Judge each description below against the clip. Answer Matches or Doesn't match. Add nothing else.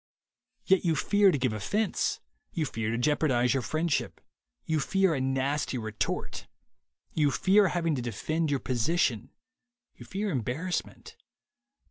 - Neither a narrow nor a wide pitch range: Doesn't match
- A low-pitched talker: Doesn't match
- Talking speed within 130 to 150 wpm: Matches